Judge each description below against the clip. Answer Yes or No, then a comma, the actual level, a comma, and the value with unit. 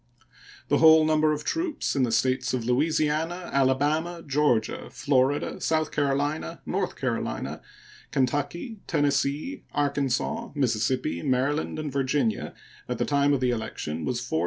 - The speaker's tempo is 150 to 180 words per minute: No, slow, 135 wpm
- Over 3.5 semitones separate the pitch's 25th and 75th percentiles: No, average, 3.2 semitones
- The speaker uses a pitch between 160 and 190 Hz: No, medium, 145 Hz